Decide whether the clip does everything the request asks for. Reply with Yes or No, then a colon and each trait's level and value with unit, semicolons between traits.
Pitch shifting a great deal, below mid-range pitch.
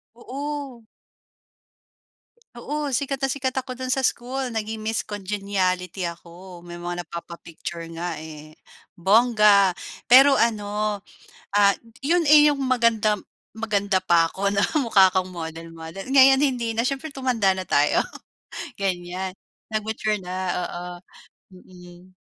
No: wide, 6.0 semitones; high, 205 Hz